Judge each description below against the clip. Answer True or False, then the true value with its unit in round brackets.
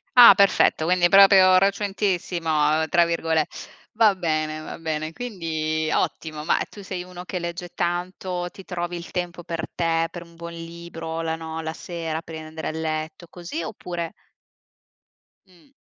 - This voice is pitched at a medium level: True (170 Hz)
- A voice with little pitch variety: True (2.0 semitones)